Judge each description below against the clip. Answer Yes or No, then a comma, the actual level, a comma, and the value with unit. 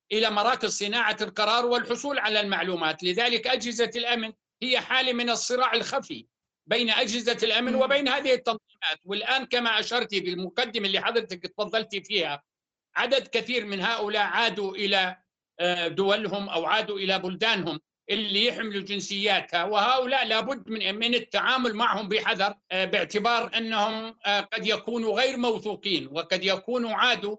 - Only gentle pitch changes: No, average, 3.0 semitones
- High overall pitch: Yes, high, 220 Hz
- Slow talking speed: No, average, 130 wpm